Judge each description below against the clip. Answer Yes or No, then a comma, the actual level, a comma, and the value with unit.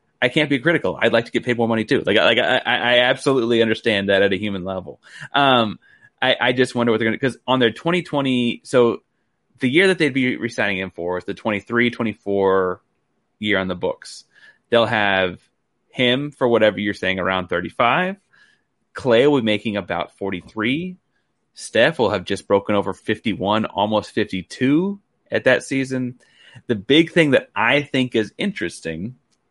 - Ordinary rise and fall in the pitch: Yes, average, 4.6 semitones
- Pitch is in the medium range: No, low, 115 Hz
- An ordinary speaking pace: Yes, average, 175 wpm